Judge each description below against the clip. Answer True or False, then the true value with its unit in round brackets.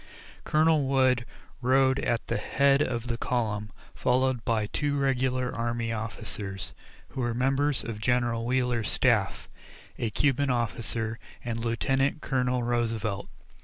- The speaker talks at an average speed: False (130 wpm)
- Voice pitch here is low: True (120 Hz)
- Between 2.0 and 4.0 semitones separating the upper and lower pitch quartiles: True (2.5 semitones)